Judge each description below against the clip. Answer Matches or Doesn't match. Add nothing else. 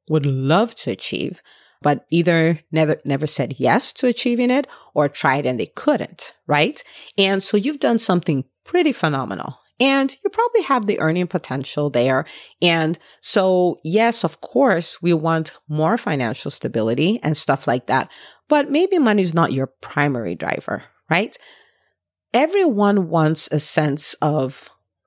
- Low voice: Doesn't match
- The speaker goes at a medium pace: Matches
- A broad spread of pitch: Matches